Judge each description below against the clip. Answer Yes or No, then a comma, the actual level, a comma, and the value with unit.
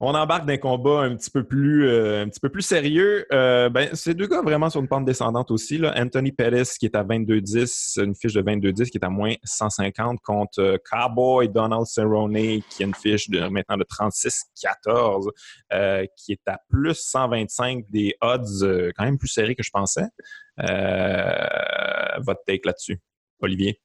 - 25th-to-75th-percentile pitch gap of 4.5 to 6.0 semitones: Yes, average, 4.9 semitones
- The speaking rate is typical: Yes, average, 185 wpm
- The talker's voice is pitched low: Yes, low, 120 Hz